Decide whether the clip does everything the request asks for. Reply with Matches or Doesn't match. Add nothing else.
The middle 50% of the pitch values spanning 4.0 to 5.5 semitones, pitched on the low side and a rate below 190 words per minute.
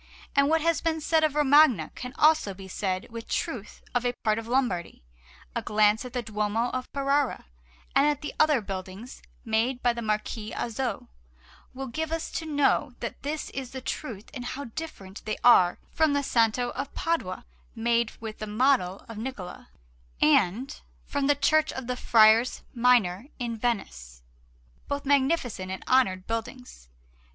Doesn't match